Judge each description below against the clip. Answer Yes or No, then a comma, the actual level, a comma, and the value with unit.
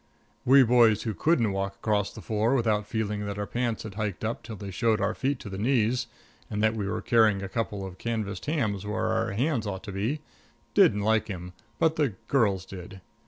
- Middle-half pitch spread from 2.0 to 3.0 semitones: Yes, average, 2.7 semitones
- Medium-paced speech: No, fast, 210 wpm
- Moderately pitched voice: No, low, 110 Hz